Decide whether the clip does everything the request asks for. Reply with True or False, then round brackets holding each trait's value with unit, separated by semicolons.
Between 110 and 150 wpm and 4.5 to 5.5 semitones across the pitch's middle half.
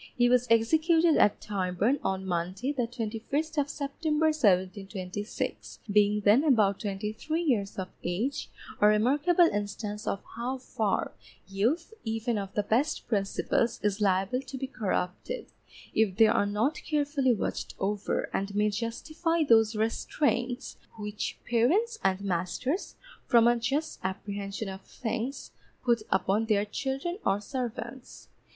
True (135 wpm; 5.2 semitones)